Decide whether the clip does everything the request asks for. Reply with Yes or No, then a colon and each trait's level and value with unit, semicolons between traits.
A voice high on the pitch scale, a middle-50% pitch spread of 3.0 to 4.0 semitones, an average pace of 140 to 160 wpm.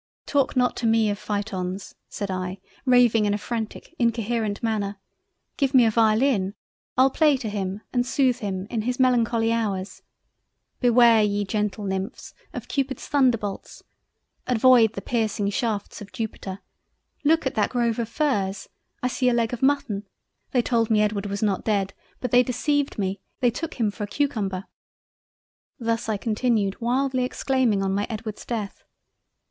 Yes: high, 225 Hz; average, 3.4 semitones; average, 150 wpm